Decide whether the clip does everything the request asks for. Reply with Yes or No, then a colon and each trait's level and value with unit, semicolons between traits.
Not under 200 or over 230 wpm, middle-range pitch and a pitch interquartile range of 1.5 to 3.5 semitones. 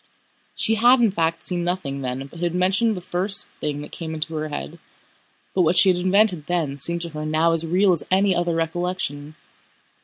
Yes: fast, 205 wpm; medium, 170 Hz; average, 3.0 semitones